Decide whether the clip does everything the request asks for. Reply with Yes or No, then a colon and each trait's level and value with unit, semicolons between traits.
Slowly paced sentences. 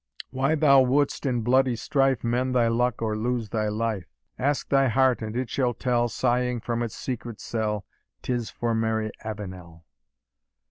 No: average, 160 wpm